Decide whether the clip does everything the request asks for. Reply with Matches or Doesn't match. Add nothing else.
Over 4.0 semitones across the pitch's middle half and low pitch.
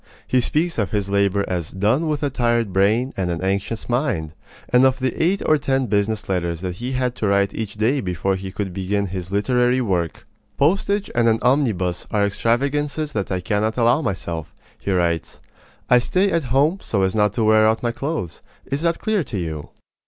Matches